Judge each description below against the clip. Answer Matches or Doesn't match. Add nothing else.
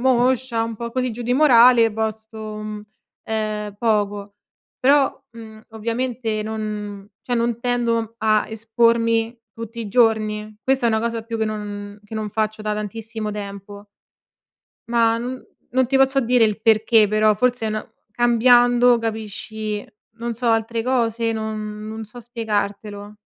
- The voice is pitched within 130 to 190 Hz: Doesn't match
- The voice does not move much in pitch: Matches